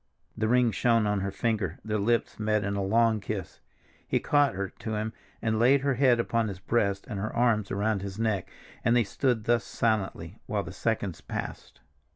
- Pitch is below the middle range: Yes, low, 110 Hz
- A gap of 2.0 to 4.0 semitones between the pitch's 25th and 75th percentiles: Yes, average, 2.8 semitones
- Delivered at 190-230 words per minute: Yes, average, 195 wpm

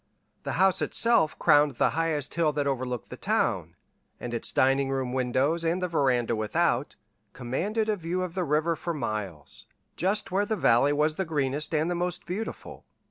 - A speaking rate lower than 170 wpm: No, average, 180 wpm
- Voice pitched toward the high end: No, medium, 150 Hz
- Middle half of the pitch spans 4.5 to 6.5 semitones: Yes, average, 5.1 semitones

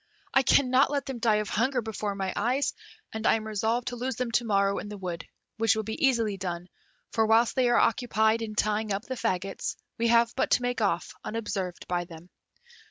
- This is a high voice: Yes, high, 220 Hz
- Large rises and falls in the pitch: No, average, 3.3 semitones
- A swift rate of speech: Yes, fast, 215 wpm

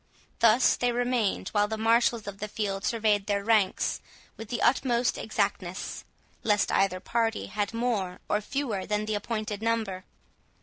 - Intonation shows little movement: Yes, narrow, 2.3 semitones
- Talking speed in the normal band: Yes, average, 150 wpm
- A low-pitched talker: No, high, 215 Hz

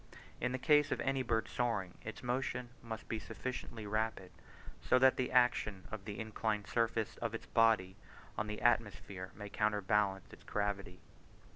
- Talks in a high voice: No, low, 110 Hz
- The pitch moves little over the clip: No, average, 3.1 semitones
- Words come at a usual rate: Yes, average, 160 wpm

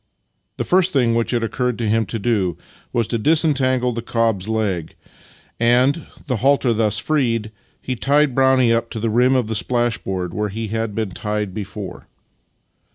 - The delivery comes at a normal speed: Yes, average, 170 wpm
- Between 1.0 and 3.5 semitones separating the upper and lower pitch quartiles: Yes, average, 3.1 semitones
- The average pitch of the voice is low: Yes, low, 115 Hz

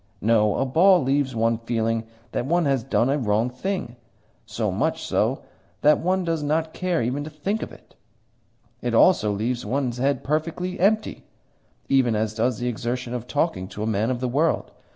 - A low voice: Yes, low, 130 Hz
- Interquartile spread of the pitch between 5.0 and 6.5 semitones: Yes, wide, 5.4 semitones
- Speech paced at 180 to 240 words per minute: Yes, average, 185 wpm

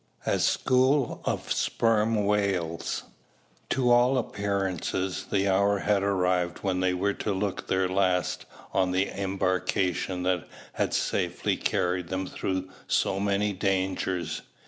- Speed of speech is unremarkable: No, slow, 125 wpm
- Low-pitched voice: Yes, very low, 95 Hz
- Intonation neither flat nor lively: No, narrow, 1.8 semitones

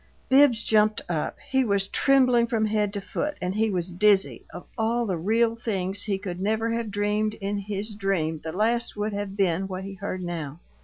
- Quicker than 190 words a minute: Yes, average, 200 wpm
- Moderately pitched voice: No, high, 205 Hz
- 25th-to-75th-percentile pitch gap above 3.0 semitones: No, average, 2.7 semitones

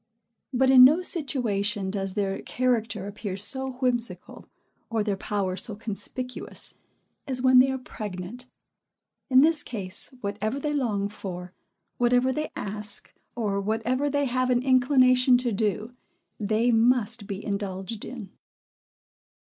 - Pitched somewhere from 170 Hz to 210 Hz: No, high, 230 Hz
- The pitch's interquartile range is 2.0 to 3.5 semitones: No, average, 4.0 semitones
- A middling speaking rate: No, slow, 130 wpm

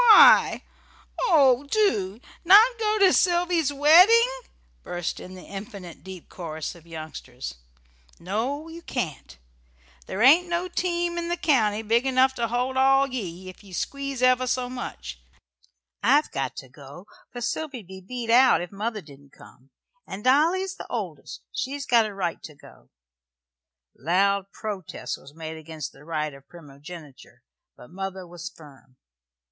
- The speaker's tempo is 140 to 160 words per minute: Yes, average, 150 wpm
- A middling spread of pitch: No, wide, 9.0 semitones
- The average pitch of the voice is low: No, high, 215 Hz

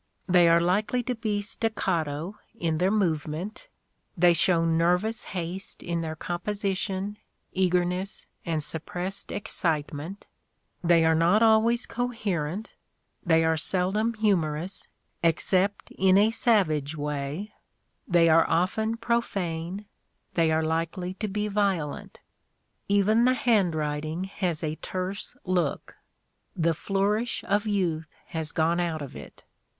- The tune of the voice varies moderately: Yes, average, 4.1 semitones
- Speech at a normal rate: No, slow, 125 wpm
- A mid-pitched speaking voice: Yes, medium, 180 Hz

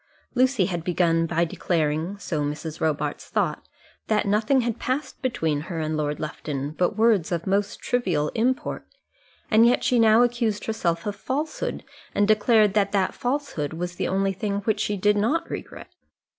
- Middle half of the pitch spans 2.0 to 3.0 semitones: No, wide, 5.6 semitones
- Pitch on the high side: Yes, high, 200 Hz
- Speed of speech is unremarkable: Yes, average, 170 wpm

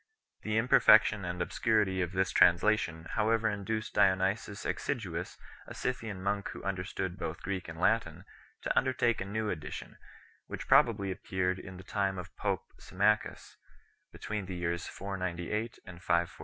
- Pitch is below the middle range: Yes, very low, 95 Hz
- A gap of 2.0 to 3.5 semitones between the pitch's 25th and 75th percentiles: Yes, average, 3.1 semitones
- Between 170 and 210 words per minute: No, average, 150 wpm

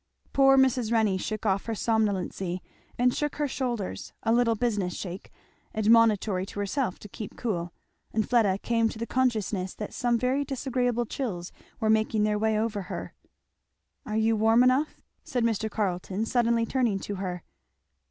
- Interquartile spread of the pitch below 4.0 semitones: Yes, average, 3.1 semitones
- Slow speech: No, average, 160 wpm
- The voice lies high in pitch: Yes, high, 220 Hz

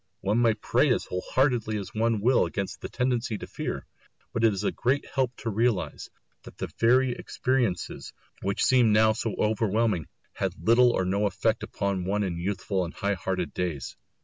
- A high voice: No, low, 110 Hz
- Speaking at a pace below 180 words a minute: No, average, 185 wpm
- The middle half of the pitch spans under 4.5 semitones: Yes, average, 3.7 semitones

